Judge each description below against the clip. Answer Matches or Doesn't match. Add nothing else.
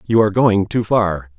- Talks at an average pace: Doesn't match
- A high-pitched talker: Doesn't match